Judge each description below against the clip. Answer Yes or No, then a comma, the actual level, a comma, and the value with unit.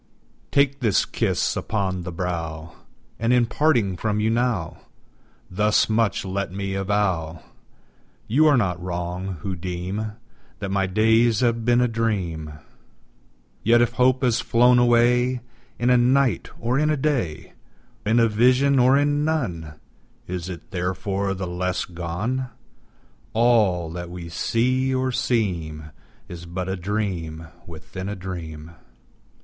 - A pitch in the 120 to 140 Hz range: No, low, 105 Hz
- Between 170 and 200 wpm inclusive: No, average, 140 wpm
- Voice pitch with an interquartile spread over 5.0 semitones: Yes, wide, 5.4 semitones